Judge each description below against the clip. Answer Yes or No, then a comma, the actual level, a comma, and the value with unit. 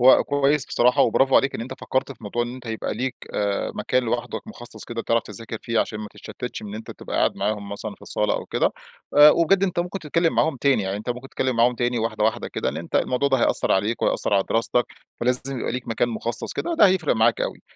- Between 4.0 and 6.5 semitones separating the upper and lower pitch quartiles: No, average, 3.3 semitones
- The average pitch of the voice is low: Yes, low, 120 Hz